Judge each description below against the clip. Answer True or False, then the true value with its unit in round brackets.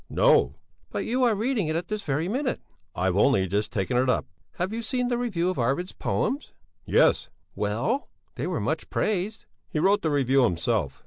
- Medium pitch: True (175 Hz)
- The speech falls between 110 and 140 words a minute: False (190 wpm)